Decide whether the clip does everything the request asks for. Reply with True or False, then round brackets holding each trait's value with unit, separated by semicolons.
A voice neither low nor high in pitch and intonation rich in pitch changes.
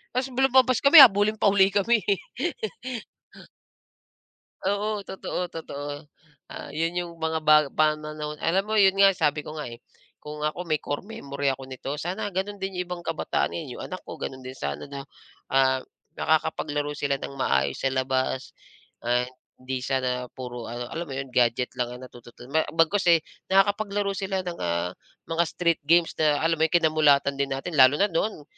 True (155 Hz; 6.1 semitones)